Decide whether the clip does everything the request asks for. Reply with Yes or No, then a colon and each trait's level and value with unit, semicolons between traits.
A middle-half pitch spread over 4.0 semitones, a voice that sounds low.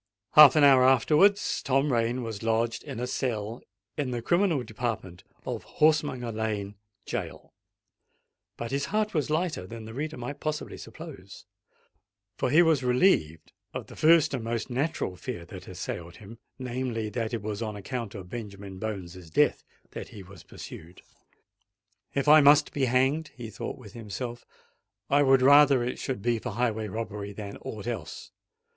Yes: average, 4.8 semitones; low, 120 Hz